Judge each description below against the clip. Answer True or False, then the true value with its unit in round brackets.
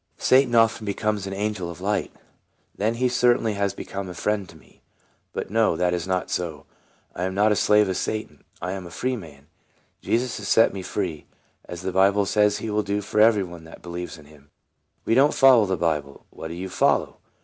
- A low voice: True (100 Hz)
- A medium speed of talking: False (225 wpm)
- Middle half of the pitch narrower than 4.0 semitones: True (3.4 semitones)